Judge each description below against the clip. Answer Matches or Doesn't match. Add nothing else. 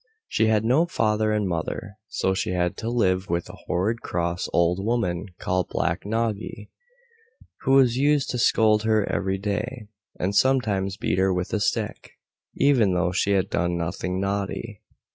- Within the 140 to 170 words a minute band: Matches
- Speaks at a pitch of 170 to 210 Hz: Doesn't match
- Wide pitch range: Doesn't match